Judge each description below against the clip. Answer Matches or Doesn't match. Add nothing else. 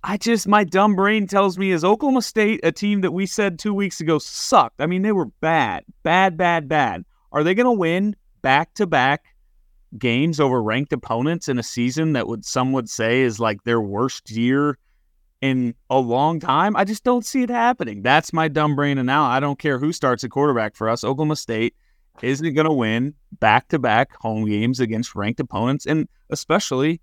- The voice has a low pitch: Doesn't match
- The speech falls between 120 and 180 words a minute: Doesn't match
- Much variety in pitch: Matches